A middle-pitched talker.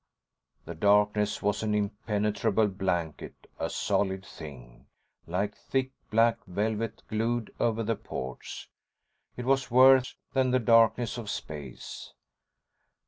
No: low, 105 Hz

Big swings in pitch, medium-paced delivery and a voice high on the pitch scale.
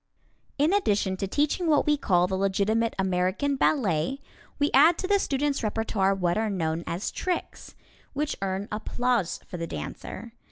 Yes: wide, 7.2 semitones; average, 160 wpm; high, 215 Hz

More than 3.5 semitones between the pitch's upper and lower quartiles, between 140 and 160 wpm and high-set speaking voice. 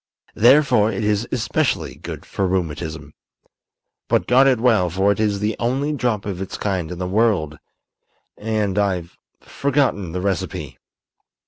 No: average, 4.3 semitones; average, 145 wpm; low, 100 Hz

